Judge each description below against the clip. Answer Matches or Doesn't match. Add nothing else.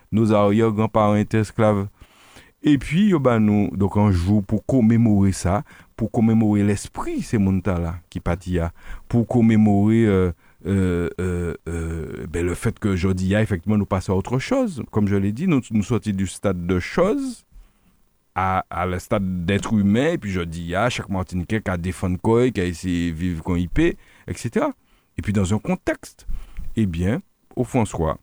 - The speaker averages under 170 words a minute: Doesn't match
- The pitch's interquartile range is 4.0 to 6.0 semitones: Doesn't match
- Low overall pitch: Matches